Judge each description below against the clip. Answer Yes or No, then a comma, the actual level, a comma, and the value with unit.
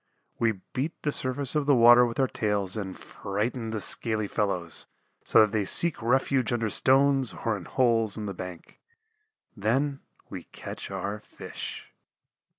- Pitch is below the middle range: Yes, low, 115 Hz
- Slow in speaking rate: No, average, 155 wpm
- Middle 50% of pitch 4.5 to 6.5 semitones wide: No, average, 4.1 semitones